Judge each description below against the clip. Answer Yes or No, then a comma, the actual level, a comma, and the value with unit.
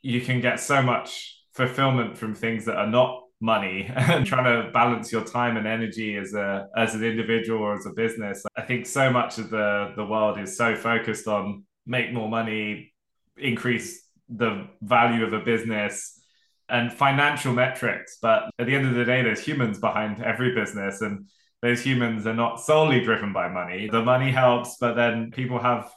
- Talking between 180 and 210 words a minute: Yes, average, 185 wpm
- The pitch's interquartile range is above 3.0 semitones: No, narrow, 2.5 semitones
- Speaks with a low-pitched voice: Yes, low, 115 Hz